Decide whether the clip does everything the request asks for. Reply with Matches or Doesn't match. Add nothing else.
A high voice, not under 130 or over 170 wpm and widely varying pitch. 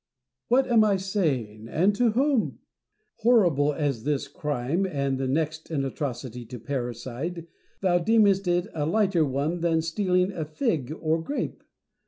Doesn't match